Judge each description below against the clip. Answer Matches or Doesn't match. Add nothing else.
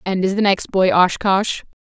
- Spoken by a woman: Matches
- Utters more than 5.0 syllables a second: Doesn't match